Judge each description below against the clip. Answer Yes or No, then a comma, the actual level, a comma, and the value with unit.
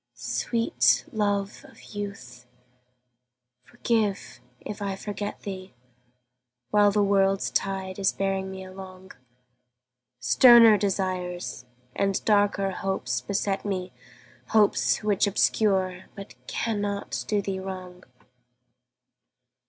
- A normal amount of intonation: No, narrow, 1.6 semitones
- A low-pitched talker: No, high, 195 Hz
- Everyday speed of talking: No, slow, 100 wpm